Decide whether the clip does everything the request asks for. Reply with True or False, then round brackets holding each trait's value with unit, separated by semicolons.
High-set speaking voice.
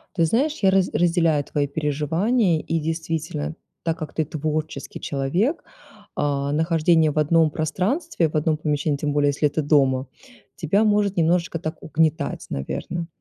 False (160 Hz)